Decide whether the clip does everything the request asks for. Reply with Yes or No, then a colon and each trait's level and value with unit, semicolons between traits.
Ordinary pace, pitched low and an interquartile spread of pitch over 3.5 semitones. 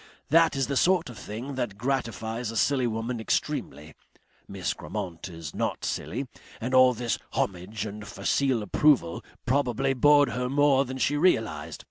Yes: average, 155 wpm; low, 125 Hz; average, 4.1 semitones